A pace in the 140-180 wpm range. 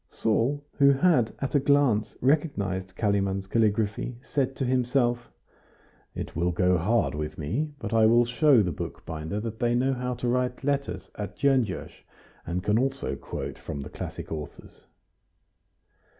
Yes: average, 150 wpm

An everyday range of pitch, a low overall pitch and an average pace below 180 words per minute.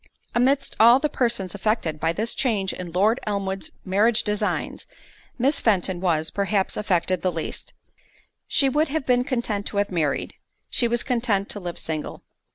No: average, 4.4 semitones; high, 205 Hz; average, 160 wpm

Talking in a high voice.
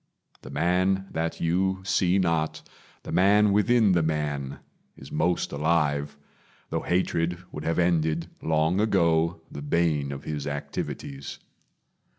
No: very low, 85 Hz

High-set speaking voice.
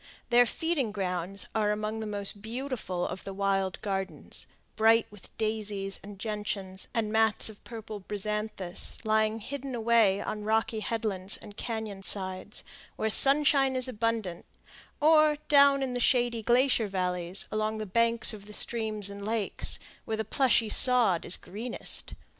Yes: high, 215 Hz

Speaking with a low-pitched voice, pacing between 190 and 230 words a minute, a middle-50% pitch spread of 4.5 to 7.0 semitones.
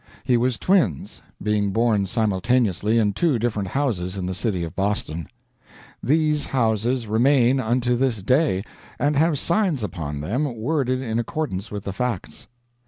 No: low, 115 Hz; average, 150 wpm; average, 4.9 semitones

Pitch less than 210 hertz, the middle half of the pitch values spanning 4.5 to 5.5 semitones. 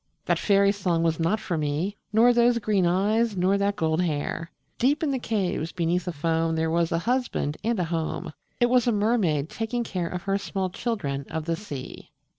Yes: medium, 185 Hz; average, 5.0 semitones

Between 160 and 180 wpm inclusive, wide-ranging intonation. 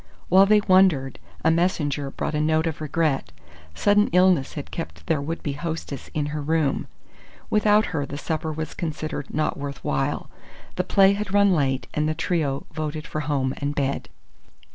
No: average, 175 wpm; average, 3.8 semitones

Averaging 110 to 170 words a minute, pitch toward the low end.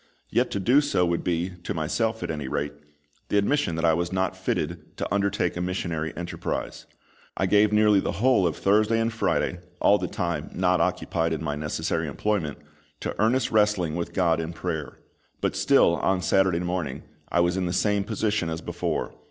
No: average, 190 wpm; very low, 90 Hz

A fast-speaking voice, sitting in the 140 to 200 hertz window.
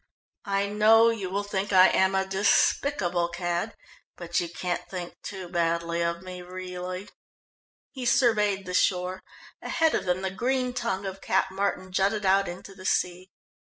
No: average, 160 wpm; high, 190 Hz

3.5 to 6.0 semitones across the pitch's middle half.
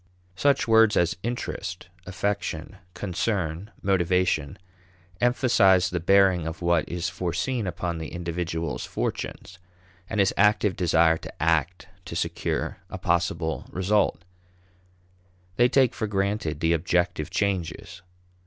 No: average, 3.1 semitones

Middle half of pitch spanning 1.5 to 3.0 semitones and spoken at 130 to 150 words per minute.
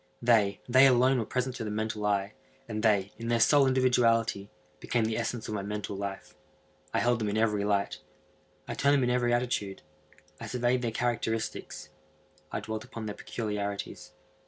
No: average, 2.7 semitones; average, 175 wpm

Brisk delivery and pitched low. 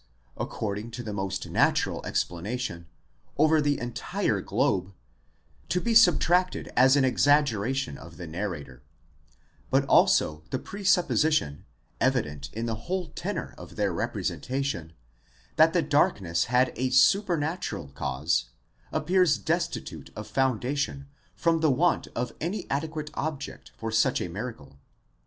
No: slow, 135 wpm; low, 130 Hz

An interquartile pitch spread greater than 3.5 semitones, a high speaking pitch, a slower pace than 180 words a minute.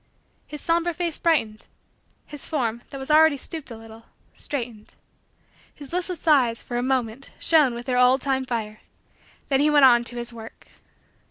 Yes: average, 4.2 semitones; very high, 265 Hz; average, 170 wpm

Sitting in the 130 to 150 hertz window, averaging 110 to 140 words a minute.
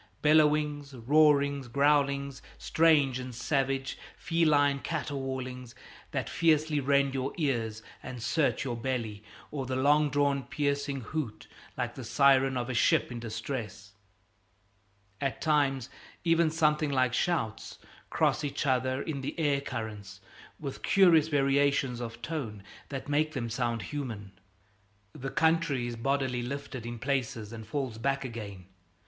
Yes: low, 135 Hz; slow, 135 wpm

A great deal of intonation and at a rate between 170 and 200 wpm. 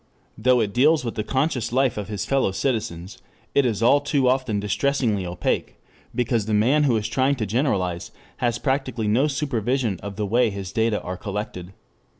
No: average, 4.3 semitones; average, 180 wpm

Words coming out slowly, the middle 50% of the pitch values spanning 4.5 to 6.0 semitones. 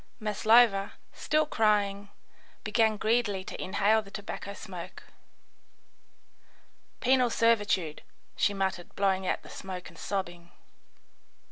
No: slow, 105 wpm; narrow, 2.5 semitones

